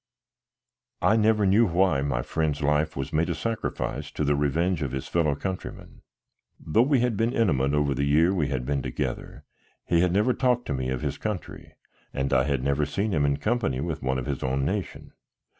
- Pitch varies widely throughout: Yes, wide, 6.6 semitones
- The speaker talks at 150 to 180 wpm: No, fast, 205 wpm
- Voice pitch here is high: No, very low, 75 Hz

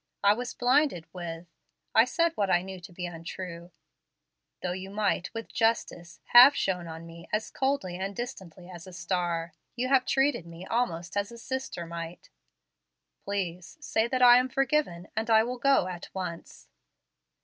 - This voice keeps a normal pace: Yes, average, 170 wpm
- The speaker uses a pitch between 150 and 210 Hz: Yes, high, 190 Hz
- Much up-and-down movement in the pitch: Yes, wide, 5.9 semitones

